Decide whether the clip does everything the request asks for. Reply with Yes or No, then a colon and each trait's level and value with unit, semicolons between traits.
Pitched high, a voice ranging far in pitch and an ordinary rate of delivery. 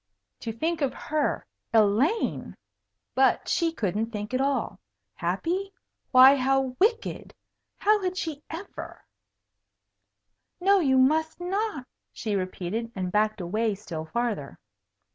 No: very high, 260 Hz; wide, 7.5 semitones; slow, 120 wpm